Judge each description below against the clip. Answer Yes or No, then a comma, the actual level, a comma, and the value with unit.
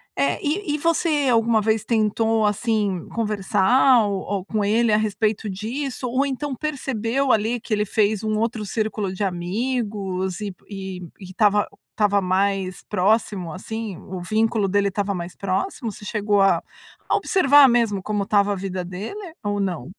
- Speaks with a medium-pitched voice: No, high, 210 Hz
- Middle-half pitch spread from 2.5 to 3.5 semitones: Yes, average, 2.9 semitones